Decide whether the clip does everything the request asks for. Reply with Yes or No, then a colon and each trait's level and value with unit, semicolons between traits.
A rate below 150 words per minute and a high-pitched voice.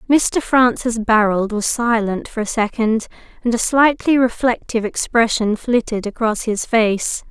Yes: average, 140 wpm; high, 230 Hz